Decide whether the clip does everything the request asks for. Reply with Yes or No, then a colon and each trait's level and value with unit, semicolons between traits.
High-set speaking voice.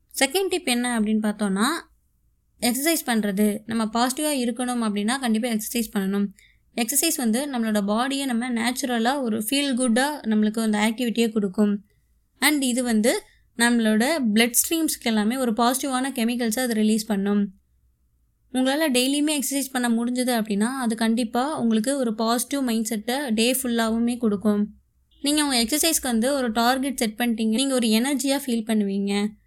Yes: high, 235 Hz